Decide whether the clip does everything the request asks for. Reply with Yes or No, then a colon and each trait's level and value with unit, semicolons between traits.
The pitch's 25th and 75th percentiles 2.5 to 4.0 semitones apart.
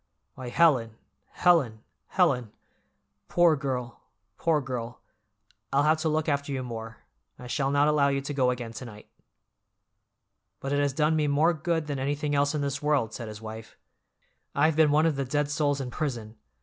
Yes: average, 3.4 semitones